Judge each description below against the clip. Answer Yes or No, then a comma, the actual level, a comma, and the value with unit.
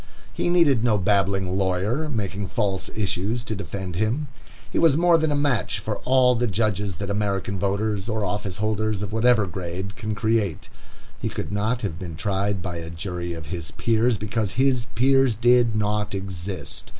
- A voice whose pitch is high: No, low, 105 Hz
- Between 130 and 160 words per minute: No, average, 175 wpm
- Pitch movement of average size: Yes, average, 3.4 semitones